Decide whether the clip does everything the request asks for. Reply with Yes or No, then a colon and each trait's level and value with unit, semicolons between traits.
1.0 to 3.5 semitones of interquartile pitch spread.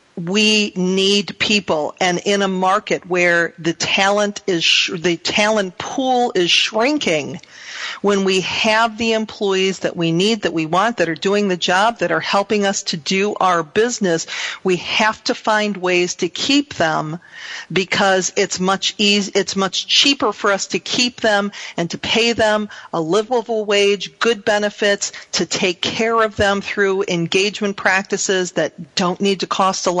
Yes: average, 2.7 semitones